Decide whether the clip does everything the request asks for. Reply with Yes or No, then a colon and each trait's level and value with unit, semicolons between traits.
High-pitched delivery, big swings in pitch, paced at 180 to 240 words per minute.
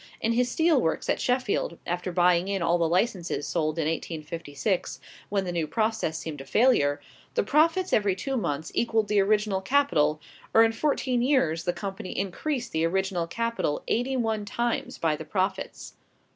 No: high, 195 Hz; wide, 5.7 semitones; average, 170 wpm